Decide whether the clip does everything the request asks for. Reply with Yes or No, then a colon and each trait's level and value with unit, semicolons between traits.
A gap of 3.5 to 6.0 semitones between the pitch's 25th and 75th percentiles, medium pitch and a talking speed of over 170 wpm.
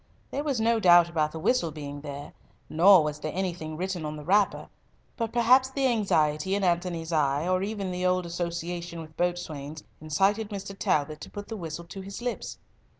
Yes: average, 4.3 semitones; medium, 175 Hz; average, 190 wpm